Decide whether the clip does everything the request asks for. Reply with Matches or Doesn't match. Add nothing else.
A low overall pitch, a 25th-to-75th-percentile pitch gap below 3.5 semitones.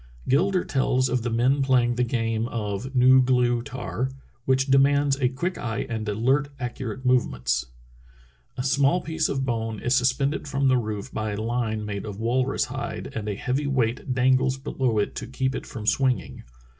Matches